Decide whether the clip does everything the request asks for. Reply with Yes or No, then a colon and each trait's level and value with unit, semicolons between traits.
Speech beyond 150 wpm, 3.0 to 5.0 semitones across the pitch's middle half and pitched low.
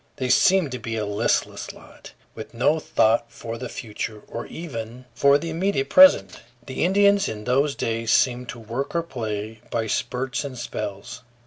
Yes: average, 175 wpm; average, 4.4 semitones; low, 125 Hz